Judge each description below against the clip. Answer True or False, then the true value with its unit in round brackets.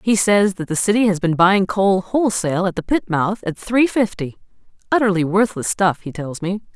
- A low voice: False (195 Hz)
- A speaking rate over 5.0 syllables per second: True (5.2 syllables/s)